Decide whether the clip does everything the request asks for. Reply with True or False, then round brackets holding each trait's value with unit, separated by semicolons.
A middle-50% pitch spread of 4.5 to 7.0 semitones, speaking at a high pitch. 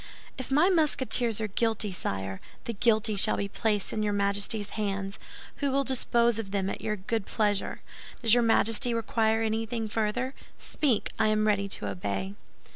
False (2.7 semitones; 220 Hz)